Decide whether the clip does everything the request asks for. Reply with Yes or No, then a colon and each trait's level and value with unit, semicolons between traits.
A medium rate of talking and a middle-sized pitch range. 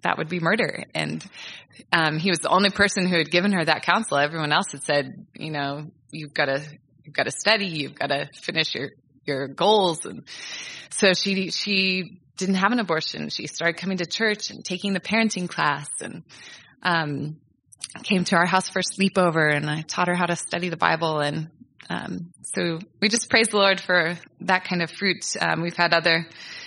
Yes: average, 195 wpm; average, 4.0 semitones